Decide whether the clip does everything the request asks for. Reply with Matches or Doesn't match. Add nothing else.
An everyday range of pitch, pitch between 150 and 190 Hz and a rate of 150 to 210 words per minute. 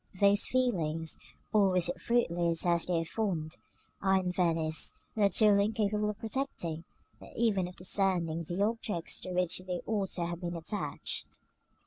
Matches